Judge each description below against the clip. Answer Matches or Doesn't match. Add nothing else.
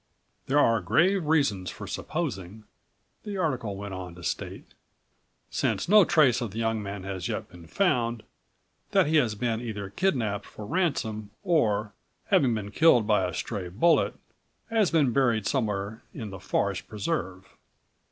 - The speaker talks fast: Doesn't match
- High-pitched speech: Doesn't match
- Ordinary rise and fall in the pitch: Doesn't match